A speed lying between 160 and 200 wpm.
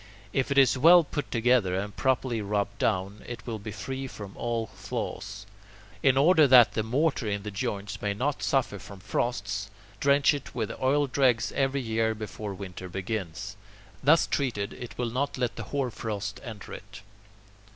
Yes: average, 170 wpm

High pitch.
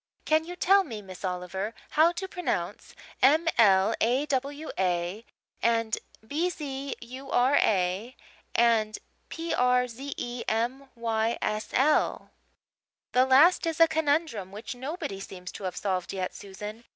Yes: high, 240 Hz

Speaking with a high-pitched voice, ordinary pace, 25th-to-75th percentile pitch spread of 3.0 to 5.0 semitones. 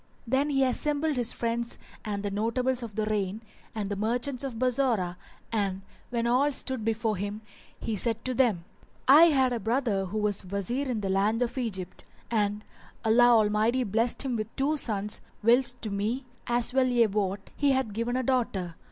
Yes: high, 230 Hz; average, 185 wpm; average, 3.5 semitones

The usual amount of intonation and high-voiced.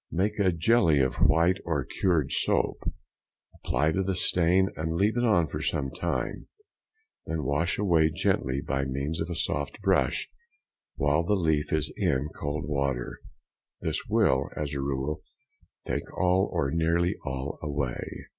No: average, 3.9 semitones; very low, 80 Hz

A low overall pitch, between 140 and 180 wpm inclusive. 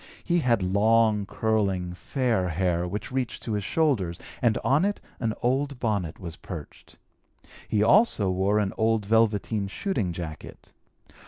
Yes: low, 105 Hz; average, 145 wpm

